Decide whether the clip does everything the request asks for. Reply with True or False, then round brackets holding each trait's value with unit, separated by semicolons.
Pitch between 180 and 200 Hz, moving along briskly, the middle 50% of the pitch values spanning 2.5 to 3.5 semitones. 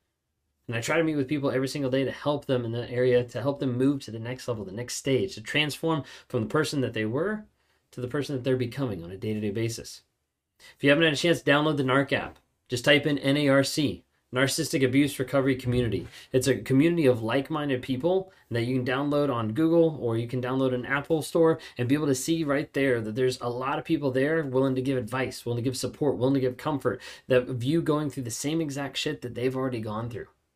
False (130 Hz; 245 wpm; 2.8 semitones)